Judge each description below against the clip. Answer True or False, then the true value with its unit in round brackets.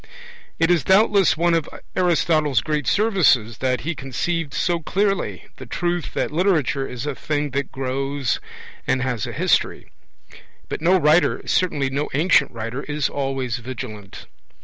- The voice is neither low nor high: True (145 Hz)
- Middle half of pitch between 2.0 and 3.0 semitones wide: False (4.7 semitones)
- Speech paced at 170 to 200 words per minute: False (150 wpm)